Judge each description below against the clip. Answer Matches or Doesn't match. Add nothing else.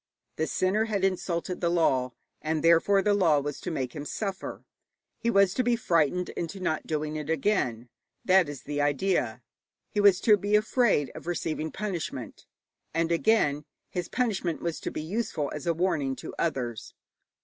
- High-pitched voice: Doesn't match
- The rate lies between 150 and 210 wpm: Matches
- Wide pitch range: Doesn't match